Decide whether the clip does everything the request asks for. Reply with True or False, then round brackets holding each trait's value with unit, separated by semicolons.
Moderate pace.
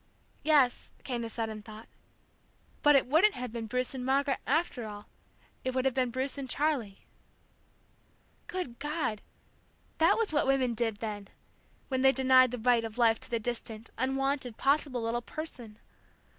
True (160 wpm)